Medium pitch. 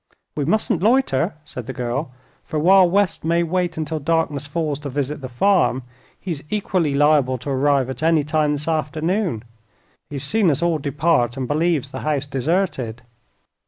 Yes: medium, 150 Hz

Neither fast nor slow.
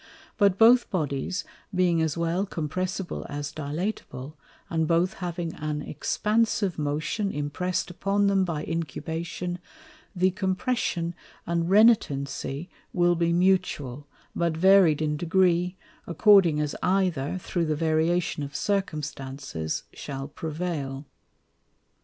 No: slow, 110 wpm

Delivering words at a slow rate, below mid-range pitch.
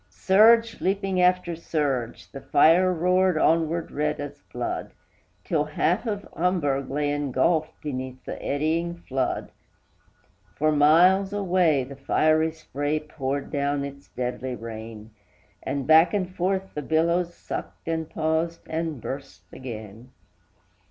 No: slow, 125 wpm; medium, 155 Hz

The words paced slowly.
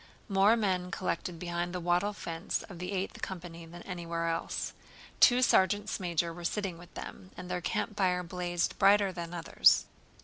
No: average, 165 wpm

